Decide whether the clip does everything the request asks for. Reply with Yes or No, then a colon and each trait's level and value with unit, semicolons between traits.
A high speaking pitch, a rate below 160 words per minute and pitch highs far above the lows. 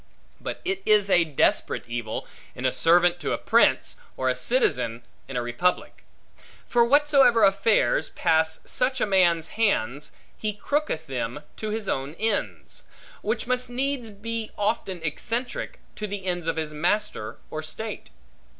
Yes: high, 195 Hz; average, 150 wpm; wide, 6.5 semitones